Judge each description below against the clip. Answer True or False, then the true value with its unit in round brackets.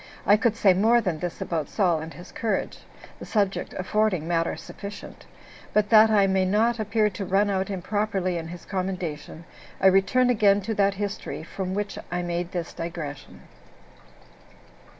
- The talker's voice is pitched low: False (195 Hz)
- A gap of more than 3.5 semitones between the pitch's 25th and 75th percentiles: False (3.1 semitones)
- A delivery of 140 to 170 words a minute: True (165 wpm)